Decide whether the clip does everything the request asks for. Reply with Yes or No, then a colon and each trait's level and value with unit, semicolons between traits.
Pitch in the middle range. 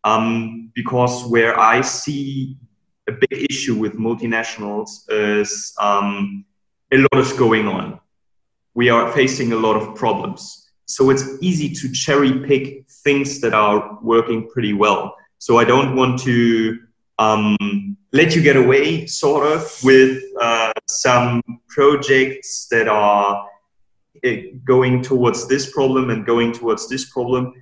No: low, 125 Hz